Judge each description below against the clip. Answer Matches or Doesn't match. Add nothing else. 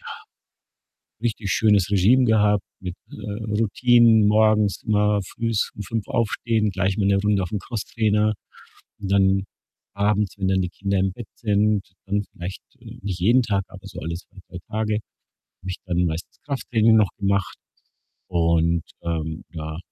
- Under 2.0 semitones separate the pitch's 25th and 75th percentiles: Doesn't match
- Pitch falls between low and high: Doesn't match